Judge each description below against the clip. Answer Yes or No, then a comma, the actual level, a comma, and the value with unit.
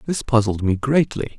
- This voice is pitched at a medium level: No, low, 120 Hz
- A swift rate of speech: No, average, 175 wpm